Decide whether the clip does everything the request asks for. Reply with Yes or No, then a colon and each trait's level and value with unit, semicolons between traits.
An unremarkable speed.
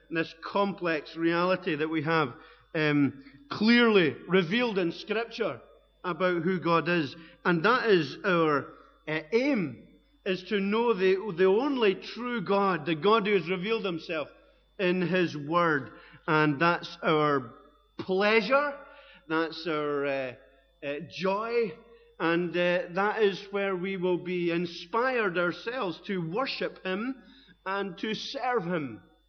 No: slow, 130 wpm